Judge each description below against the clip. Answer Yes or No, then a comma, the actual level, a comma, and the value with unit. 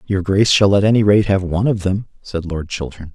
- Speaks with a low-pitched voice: Yes, very low, 95 Hz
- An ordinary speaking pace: No, fast, 250 wpm